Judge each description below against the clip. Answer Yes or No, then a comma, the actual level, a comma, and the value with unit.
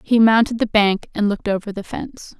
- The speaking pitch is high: Yes, high, 215 Hz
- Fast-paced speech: Yes, fast, 225 wpm